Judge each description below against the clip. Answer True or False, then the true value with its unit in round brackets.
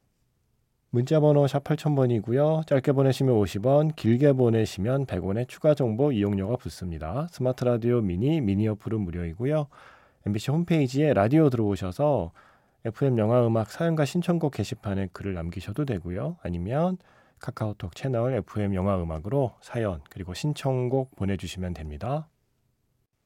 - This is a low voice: True (120 Hz)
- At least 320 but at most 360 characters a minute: True (330 characters per minute)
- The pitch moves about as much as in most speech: False (5.9 semitones)